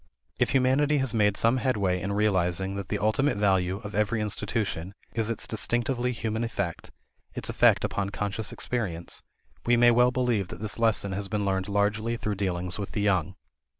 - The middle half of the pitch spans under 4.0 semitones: Yes, average, 3.0 semitones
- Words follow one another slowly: No, average, 180 wpm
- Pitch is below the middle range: Yes, low, 105 Hz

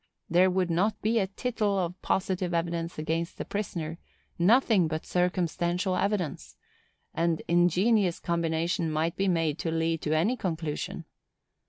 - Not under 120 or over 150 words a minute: Yes, average, 140 wpm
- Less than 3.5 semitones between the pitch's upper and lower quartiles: Yes, narrow, 2.6 semitones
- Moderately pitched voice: Yes, medium, 175 Hz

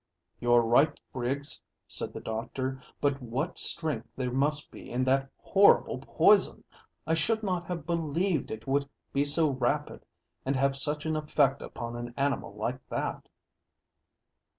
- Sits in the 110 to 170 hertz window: Yes, medium, 140 Hz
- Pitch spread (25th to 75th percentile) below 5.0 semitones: Yes, average, 3.4 semitones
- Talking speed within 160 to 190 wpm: No, average, 150 wpm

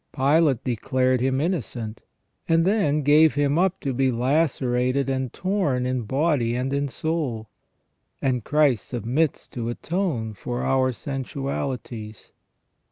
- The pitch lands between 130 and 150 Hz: Yes, low, 135 Hz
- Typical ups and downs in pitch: Yes, average, 3.5 semitones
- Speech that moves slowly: Yes, slow, 125 wpm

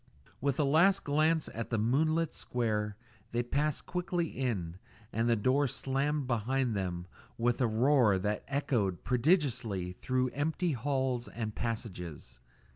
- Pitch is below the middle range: Yes, low, 125 Hz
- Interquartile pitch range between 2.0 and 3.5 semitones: No, average, 5.0 semitones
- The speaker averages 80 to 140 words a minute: Yes, slow, 135 wpm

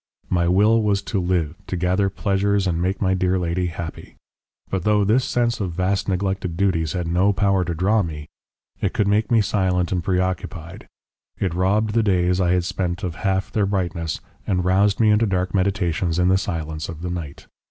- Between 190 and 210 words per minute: Yes, average, 195 wpm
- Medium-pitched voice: No, very low, 95 Hz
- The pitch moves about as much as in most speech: No, narrow, 2.2 semitones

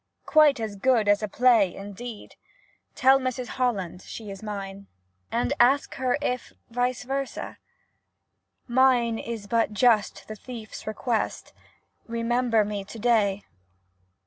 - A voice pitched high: Yes, high, 230 Hz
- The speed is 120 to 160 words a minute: Yes, slow, 135 wpm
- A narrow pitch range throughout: No, average, 3.4 semitones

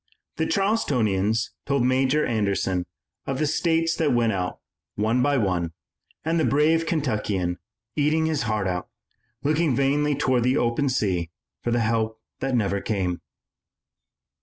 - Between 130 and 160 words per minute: Yes, average, 140 wpm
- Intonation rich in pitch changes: Yes, wide, 6.1 semitones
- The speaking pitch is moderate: No, low, 125 Hz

